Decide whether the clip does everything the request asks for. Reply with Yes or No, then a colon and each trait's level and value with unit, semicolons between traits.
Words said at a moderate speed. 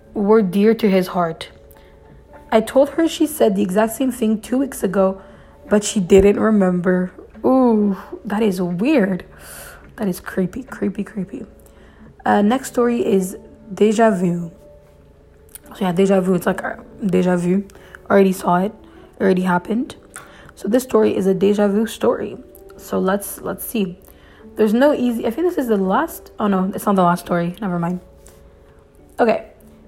Yes: average, 165 wpm